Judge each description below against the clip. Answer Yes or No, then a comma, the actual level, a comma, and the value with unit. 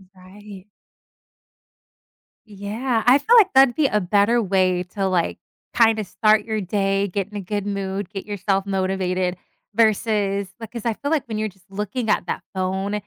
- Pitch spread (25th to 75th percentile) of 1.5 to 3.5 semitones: Yes, narrow, 2.5 semitones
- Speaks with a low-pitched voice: No, high, 205 Hz